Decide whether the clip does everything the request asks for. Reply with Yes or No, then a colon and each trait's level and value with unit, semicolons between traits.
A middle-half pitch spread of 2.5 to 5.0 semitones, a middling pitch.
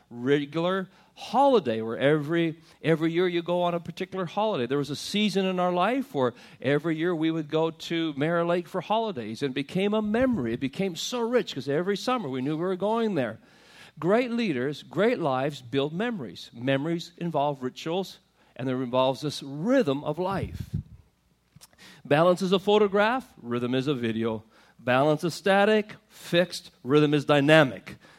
No: wide, 5.5 semitones; medium, 170 Hz